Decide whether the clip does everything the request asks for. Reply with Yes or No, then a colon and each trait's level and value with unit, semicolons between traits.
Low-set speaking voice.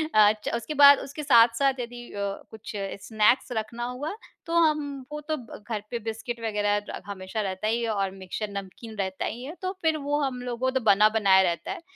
No: high, 225 Hz